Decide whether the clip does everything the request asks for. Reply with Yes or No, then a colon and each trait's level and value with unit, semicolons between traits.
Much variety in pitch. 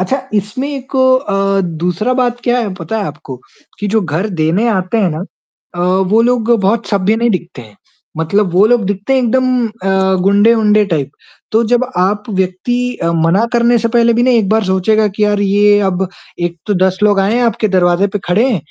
No: average, 3.8 semitones